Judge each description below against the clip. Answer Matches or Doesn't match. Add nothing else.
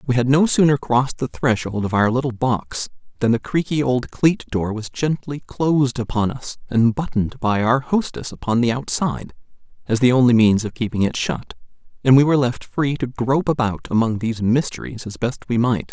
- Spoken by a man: Matches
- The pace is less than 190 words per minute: Doesn't match